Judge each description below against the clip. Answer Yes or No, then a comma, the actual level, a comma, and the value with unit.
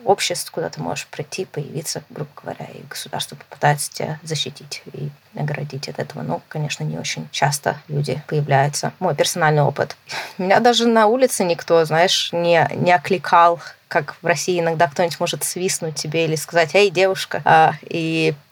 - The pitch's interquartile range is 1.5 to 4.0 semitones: Yes, average, 3.2 semitones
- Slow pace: No, fast, 160 wpm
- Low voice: No, medium, 165 Hz